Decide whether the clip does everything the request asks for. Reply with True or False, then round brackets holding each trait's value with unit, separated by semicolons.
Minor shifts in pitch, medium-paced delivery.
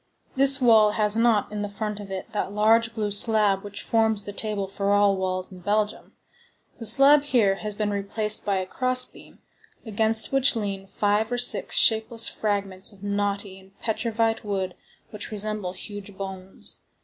True (2.0 semitones; 170 wpm)